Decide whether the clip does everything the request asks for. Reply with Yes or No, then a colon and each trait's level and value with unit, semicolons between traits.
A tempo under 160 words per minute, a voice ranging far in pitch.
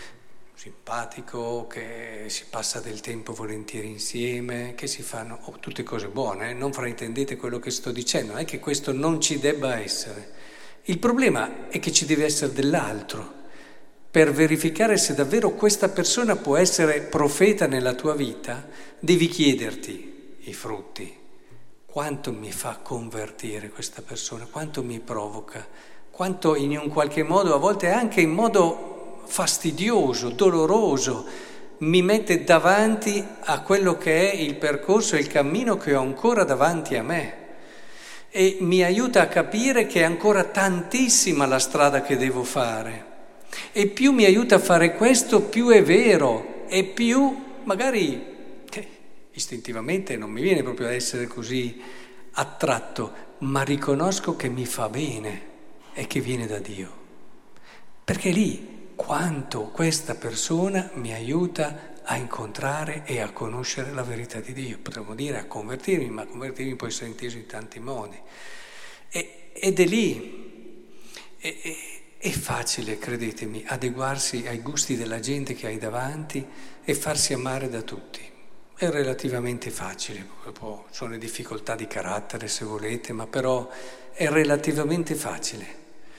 Yes: average, 145 wpm; wide, 6.5 semitones